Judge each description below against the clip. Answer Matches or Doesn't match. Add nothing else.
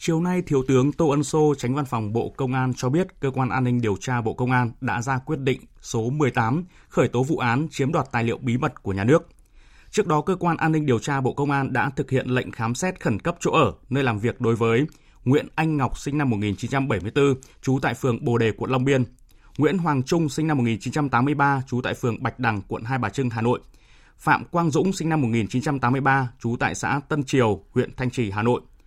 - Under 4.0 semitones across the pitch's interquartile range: Matches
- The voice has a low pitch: Matches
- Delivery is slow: Doesn't match